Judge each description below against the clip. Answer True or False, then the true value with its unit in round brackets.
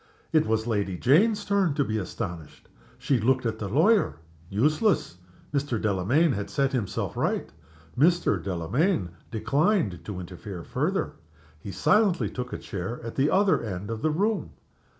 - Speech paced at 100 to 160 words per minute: True (150 wpm)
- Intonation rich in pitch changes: True (8.1 semitones)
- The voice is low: True (125 Hz)